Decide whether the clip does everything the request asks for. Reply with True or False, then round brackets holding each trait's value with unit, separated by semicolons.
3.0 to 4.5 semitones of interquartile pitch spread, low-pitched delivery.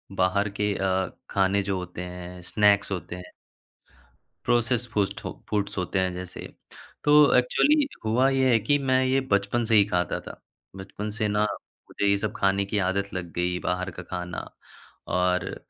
True (3.3 semitones; 100 Hz)